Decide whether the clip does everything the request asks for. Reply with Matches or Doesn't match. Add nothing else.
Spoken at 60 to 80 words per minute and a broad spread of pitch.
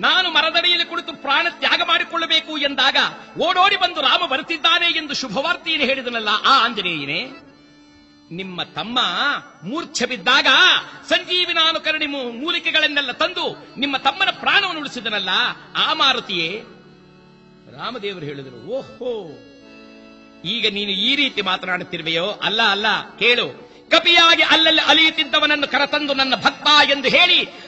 Doesn't match